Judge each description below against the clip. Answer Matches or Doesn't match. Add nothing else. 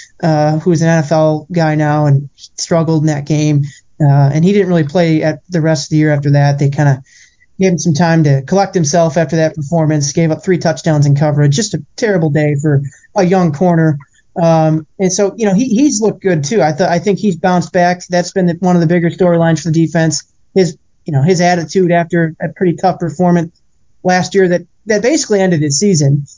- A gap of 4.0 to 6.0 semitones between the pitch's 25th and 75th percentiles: Doesn't match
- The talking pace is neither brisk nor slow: Doesn't match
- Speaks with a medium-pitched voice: Matches